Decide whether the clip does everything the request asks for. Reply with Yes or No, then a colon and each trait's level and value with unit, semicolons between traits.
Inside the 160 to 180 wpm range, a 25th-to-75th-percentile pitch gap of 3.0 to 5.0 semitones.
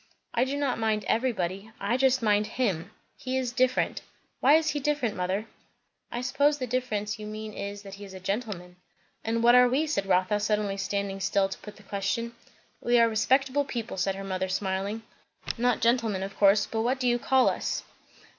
No: average, 195 wpm; average, 4.2 semitones